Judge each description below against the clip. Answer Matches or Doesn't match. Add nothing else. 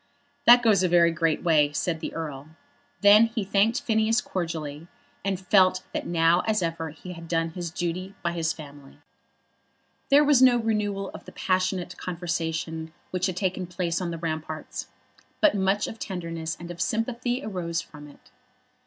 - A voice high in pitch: Doesn't match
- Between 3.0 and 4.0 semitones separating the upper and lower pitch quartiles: Matches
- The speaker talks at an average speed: Matches